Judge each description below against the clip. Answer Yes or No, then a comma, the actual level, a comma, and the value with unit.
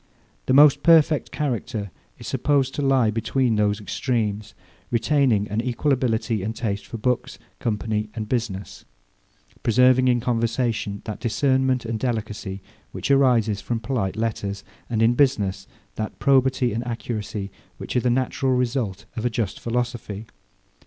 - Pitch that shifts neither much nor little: Yes, average, 3.2 semitones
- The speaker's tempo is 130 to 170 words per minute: Yes, average, 145 wpm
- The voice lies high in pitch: No, low, 115 Hz